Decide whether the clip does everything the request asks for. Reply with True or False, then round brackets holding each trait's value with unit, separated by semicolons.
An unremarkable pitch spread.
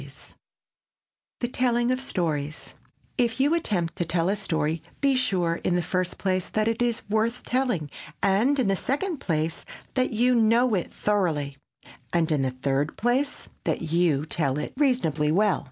False (7.1 semitones)